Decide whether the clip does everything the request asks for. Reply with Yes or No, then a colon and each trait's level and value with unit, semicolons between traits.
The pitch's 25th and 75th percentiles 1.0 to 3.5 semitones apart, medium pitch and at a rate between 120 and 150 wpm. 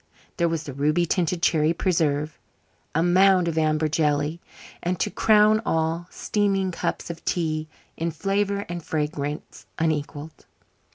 Yes: average, 2.8 semitones; medium, 165 Hz; slow, 135 wpm